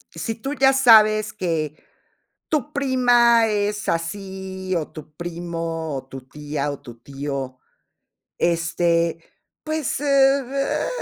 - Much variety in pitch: Yes, wide, 7.2 semitones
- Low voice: No, medium, 185 Hz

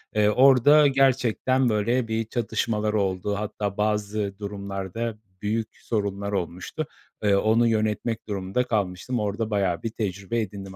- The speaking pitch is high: No, low, 105 Hz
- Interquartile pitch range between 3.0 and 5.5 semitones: No, narrow, 2.6 semitones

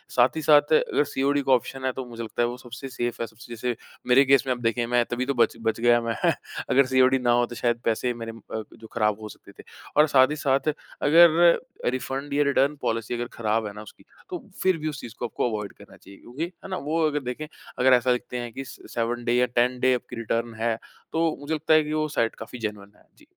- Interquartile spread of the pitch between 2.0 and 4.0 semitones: Yes, average, 3.4 semitones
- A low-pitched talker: Yes, low, 125 Hz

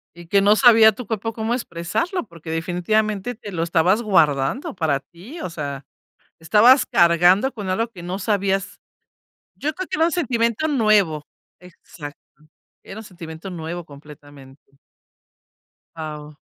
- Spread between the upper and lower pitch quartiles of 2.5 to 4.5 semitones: No, wide, 5.5 semitones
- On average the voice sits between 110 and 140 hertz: No, medium, 185 Hz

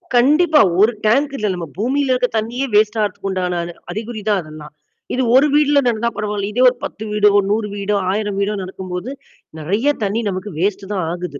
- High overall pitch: Yes, high, 210 Hz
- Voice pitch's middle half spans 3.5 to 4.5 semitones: Yes, average, 4.1 semitones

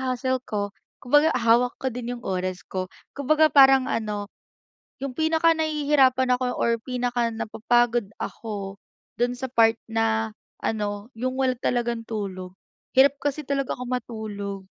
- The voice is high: Yes, high, 245 Hz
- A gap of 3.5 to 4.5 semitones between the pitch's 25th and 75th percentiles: No, average, 3.0 semitones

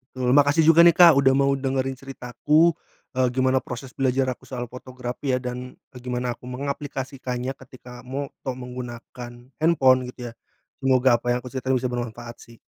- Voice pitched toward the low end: Yes, low, 130 Hz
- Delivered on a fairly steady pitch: Yes, narrow, 1.6 semitones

